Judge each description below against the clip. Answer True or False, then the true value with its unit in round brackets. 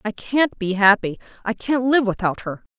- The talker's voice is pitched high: True (220 Hz)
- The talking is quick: False (170 wpm)